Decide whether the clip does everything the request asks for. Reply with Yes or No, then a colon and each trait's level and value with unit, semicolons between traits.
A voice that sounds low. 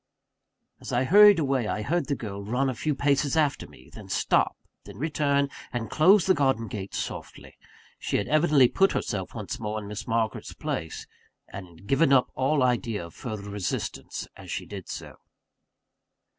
Yes: low, 125 Hz